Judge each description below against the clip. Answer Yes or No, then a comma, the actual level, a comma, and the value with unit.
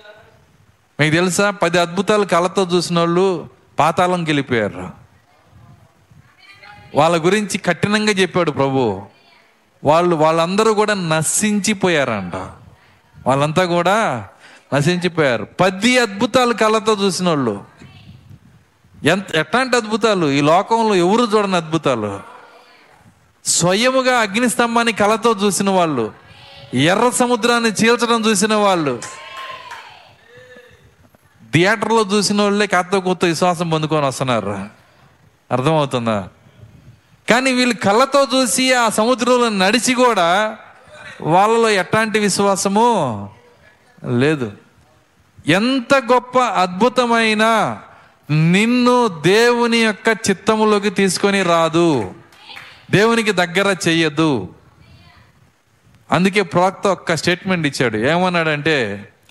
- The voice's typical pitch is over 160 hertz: Yes, high, 190 Hz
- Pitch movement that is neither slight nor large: No, wide, 6.1 semitones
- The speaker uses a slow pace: No, average, 85 wpm